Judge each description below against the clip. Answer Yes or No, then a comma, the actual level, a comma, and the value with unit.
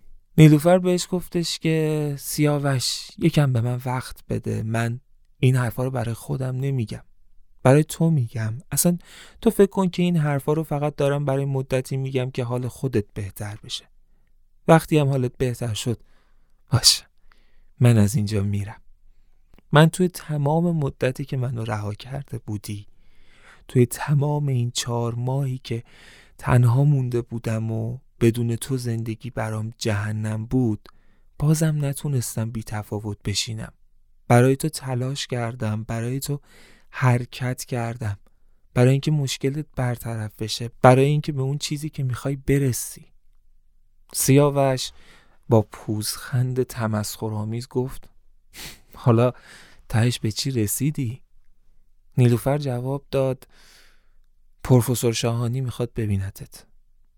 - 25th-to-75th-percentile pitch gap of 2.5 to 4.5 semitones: Yes, average, 3.9 semitones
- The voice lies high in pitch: No, low, 125 Hz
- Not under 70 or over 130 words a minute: Yes, average, 125 wpm